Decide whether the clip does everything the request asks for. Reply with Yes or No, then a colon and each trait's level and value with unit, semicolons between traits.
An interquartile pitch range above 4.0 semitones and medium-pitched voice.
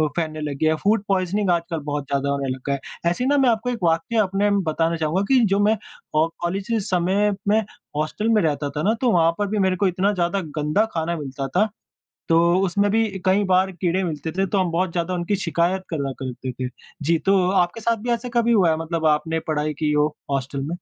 Yes: average, 4.6 semitones; medium, 175 Hz